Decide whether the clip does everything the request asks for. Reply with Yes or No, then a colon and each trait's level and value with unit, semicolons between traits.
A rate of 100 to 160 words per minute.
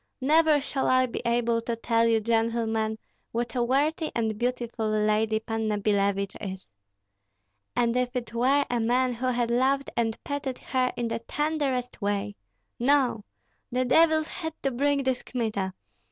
Yes: average, 155 wpm